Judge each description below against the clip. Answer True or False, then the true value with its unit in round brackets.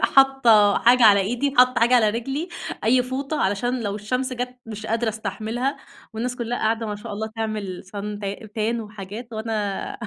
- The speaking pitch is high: True (225 Hz)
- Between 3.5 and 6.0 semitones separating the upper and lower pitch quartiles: False (2.9 semitones)